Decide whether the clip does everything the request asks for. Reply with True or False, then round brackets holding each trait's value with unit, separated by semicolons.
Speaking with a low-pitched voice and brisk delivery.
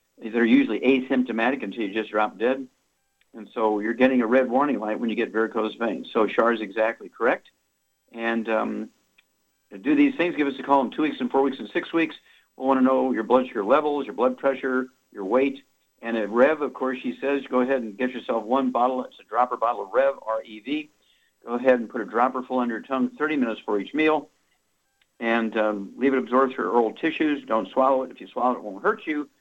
True (125 Hz; 235 wpm)